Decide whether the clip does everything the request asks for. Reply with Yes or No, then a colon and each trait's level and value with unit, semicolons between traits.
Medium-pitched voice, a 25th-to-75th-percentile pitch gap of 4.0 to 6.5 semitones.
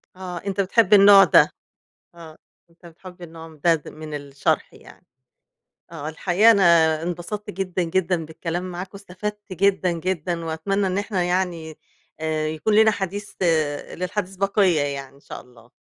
No: medium, 180 Hz; average, 3.4 semitones